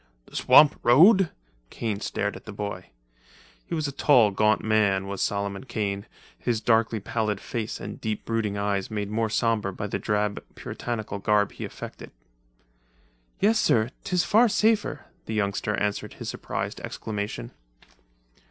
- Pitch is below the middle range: Yes, low, 110 Hz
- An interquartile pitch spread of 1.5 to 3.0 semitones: Yes, average, 2.7 semitones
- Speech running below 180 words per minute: Yes, average, 150 wpm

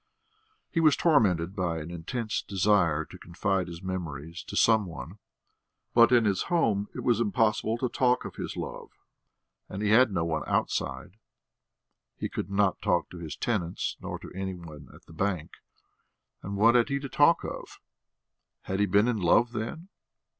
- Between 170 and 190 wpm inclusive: Yes, average, 175 wpm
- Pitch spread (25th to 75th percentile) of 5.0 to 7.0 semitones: Yes, average, 5.3 semitones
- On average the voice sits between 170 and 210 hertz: No, low, 100 Hz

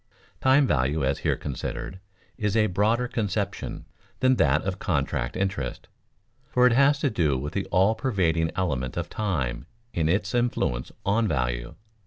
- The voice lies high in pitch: No, very low, 95 Hz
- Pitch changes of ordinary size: No, wide, 7.8 semitones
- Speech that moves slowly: No, average, 155 wpm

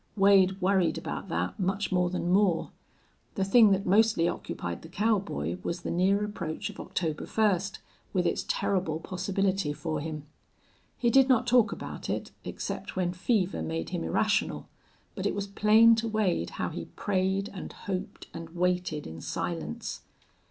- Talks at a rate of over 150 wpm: Yes, average, 160 wpm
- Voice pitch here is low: No, high, 190 Hz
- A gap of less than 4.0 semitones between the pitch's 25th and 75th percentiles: Yes, average, 3.4 semitones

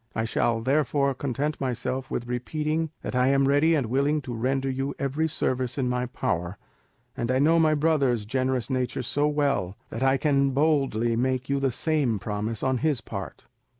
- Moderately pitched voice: No, low, 130 Hz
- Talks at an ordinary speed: Yes, average, 185 wpm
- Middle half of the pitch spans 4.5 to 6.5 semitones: No, average, 2.7 semitones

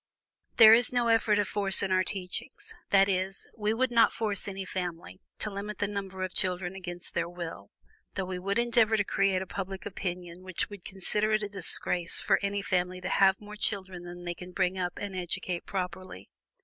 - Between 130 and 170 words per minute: No, average, 200 wpm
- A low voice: No, high, 190 Hz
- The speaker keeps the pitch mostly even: Yes, narrow, 2.2 semitones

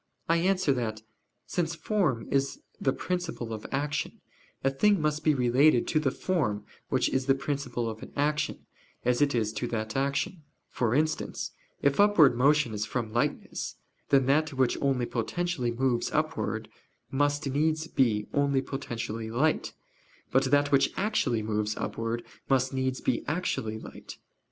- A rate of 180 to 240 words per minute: No, average, 155 wpm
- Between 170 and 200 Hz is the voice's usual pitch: No, low, 135 Hz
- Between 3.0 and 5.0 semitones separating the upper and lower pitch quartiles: Yes, average, 4.3 semitones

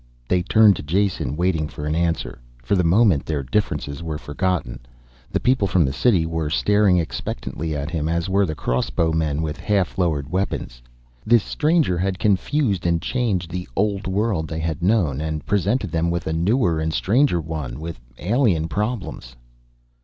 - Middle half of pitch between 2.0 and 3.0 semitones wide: No, average, 4.4 semitones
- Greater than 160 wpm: Yes, average, 170 wpm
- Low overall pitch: Yes, very low, 85 Hz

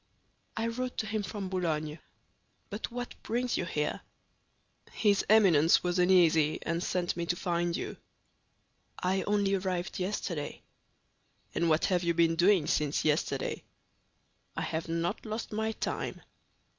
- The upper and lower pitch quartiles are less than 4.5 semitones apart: Yes, average, 3.7 semitones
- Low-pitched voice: No, medium, 180 Hz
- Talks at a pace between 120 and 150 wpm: Yes, average, 140 wpm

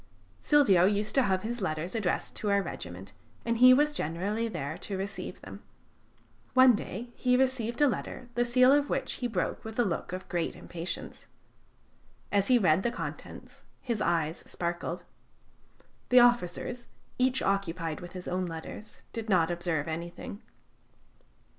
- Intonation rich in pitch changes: Yes, wide, 5.8 semitones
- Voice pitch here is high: Yes, high, 200 Hz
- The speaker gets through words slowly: No, average, 155 wpm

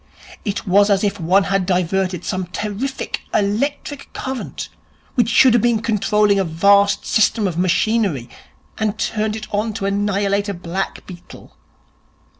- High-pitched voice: Yes, high, 200 Hz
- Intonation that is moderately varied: No, narrow, 2.2 semitones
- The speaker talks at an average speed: Yes, average, 145 wpm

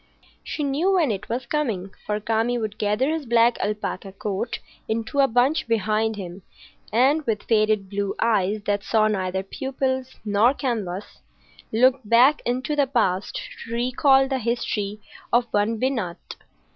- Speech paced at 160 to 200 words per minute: No, average, 150 wpm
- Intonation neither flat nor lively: Yes, average, 4.0 semitones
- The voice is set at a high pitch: Yes, high, 230 Hz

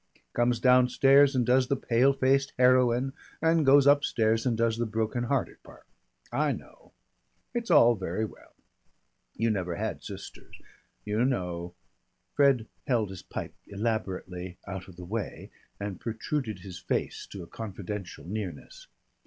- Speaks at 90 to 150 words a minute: Yes, average, 145 wpm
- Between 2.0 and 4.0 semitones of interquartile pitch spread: No, average, 5.0 semitones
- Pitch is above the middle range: No, low, 115 Hz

